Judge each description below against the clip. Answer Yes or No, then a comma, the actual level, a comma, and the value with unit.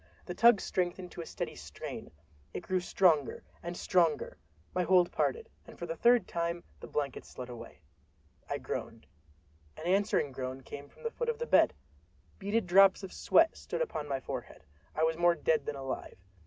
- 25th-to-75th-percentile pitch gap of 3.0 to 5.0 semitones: No, wide, 5.6 semitones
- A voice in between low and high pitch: Yes, medium, 175 Hz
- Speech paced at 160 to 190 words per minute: Yes, average, 180 wpm